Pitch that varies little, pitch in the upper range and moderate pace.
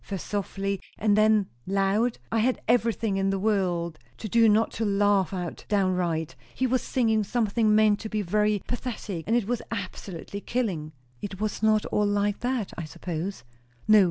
Yes: narrow, 2.3 semitones; high, 205 Hz; average, 175 wpm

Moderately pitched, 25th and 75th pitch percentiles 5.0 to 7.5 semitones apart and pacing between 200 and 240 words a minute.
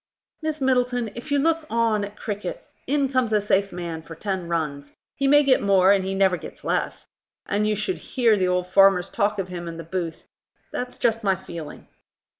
No: high, 200 Hz; wide, 5.4 semitones; fast, 205 wpm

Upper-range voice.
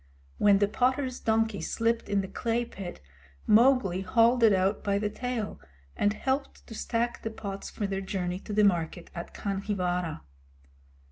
Yes: high, 205 Hz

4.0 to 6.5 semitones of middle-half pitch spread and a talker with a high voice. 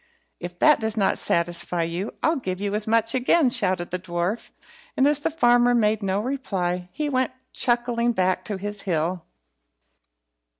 Yes: average, 5.1 semitones; high, 210 Hz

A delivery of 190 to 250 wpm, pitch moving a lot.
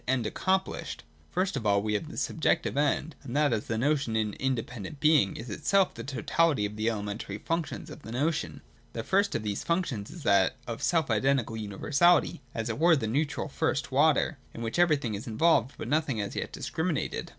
Yes: average, 195 wpm; wide, 6.3 semitones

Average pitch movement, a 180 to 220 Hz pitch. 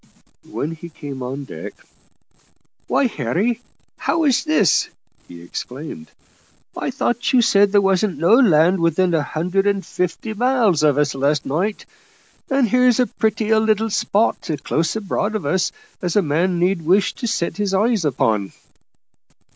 No: wide, 5.7 semitones; high, 190 Hz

